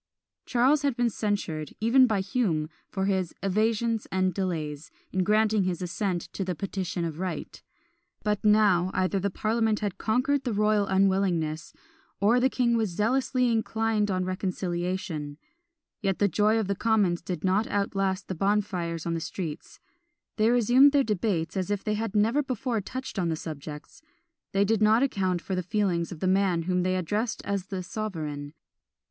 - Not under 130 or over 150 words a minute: No, average, 170 wpm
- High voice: Yes, high, 195 Hz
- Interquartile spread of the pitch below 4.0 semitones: Yes, average, 3.4 semitones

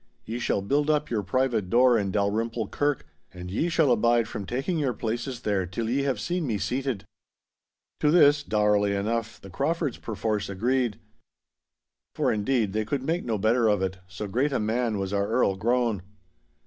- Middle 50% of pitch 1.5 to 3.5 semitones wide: No, average, 4.5 semitones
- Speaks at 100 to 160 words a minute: No, average, 180 wpm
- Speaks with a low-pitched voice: Yes, low, 115 Hz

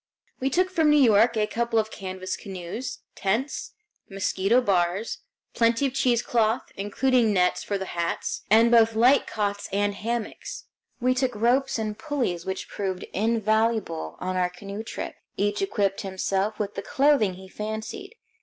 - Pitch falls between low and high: No, high, 220 Hz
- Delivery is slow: No, average, 155 wpm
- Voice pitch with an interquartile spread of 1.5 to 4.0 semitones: Yes, average, 3.7 semitones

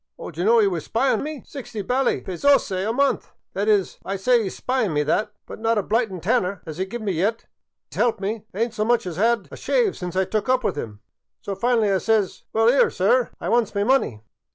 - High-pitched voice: Yes, high, 215 Hz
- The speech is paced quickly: Yes, fast, 260 wpm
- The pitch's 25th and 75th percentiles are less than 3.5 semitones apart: No, average, 4.0 semitones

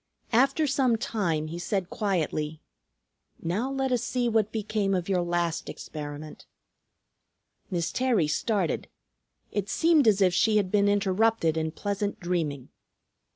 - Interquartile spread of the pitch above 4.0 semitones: Yes, average, 4.8 semitones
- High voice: Yes, high, 195 Hz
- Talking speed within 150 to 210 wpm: No, slow, 135 wpm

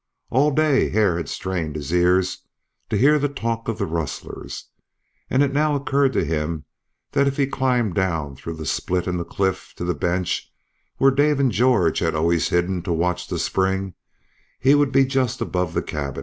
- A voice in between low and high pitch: No, very low, 95 Hz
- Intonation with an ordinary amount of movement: No, wide, 7.8 semitones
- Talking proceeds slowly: No, average, 190 wpm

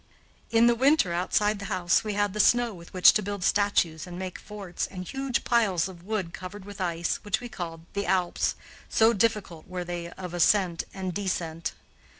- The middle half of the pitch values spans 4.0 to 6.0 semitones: No, average, 3.1 semitones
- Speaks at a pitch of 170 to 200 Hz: Yes, high, 190 Hz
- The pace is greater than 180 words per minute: Yes, average, 190 wpm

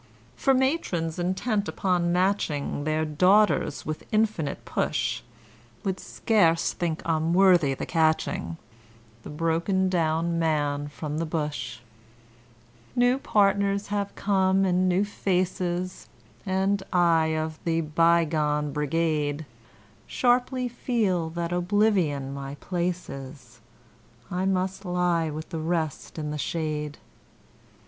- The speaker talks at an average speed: No, slow, 115 wpm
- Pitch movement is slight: No, average, 3.6 semitones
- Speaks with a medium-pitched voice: Yes, medium, 170 Hz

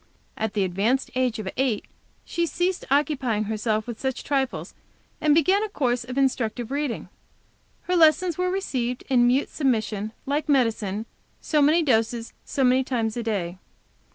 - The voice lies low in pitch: No, very high, 255 Hz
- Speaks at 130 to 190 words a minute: Yes, average, 155 wpm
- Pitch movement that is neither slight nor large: Yes, average, 4.8 semitones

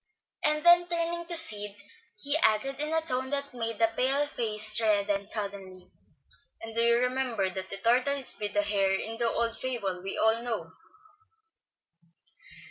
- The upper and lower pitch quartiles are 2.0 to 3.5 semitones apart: No, average, 4.8 semitones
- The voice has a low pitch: No, high, 230 Hz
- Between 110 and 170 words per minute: Yes, average, 155 wpm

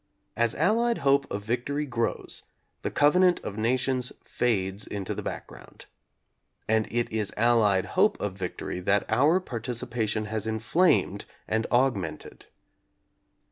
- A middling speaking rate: No, slow, 125 wpm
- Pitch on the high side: No, low, 115 Hz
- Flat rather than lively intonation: No, average, 4.2 semitones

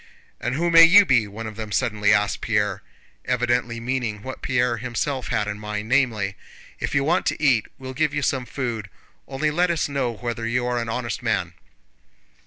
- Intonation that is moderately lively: Yes, average, 3.6 semitones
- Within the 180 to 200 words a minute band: Yes, average, 195 wpm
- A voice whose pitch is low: Yes, low, 120 Hz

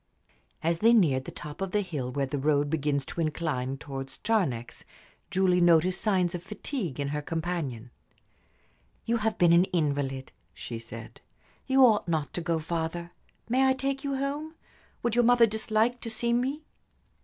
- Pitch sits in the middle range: Yes, medium, 175 Hz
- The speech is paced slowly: No, average, 170 wpm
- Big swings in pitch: Yes, wide, 7.8 semitones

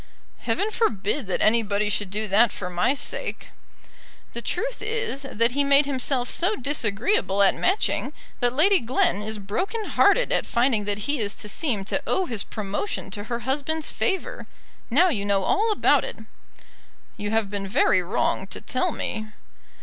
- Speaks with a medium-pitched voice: No, high, 235 Hz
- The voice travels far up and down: Yes, wide, 6.9 semitones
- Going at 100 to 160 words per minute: No, average, 170 wpm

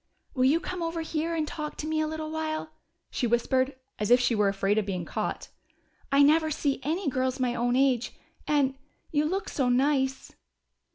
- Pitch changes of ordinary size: Yes, average, 4.0 semitones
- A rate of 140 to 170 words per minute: No, average, 190 wpm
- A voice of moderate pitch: No, very high, 280 Hz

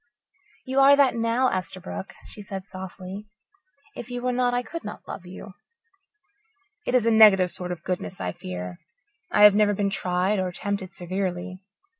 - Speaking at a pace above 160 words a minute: Yes, average, 170 wpm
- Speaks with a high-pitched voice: Yes, high, 195 Hz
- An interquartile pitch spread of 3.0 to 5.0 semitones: Yes, average, 4.0 semitones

